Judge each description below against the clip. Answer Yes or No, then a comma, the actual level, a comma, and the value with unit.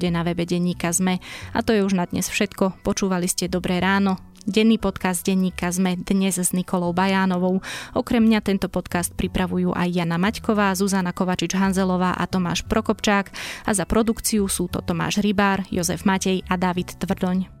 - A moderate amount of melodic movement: No, narrow, 1.8 semitones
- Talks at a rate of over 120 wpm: Yes, fast, 165 wpm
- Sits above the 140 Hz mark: Yes, high, 190 Hz